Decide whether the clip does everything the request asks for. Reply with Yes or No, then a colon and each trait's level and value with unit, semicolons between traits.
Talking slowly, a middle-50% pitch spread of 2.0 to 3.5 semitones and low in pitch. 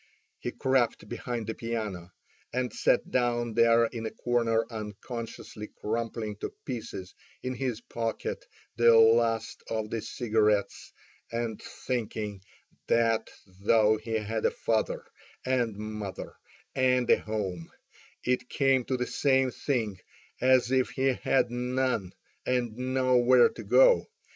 Yes: slow, 130 wpm; narrow, 2.5 semitones; low, 115 Hz